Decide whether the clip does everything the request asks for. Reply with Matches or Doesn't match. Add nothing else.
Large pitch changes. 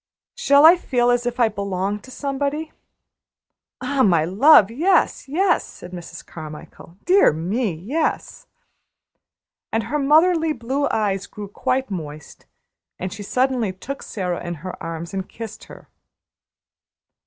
Matches